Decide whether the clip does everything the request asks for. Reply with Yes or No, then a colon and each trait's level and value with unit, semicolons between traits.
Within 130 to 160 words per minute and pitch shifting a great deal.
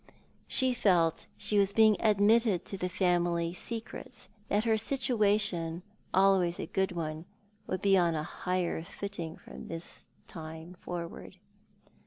No: average, 140 wpm; average, 3.4 semitones